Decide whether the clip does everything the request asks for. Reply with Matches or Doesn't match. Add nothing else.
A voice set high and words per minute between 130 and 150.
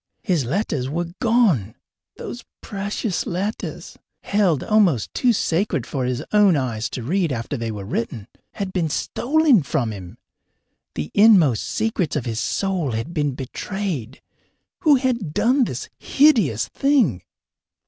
Doesn't match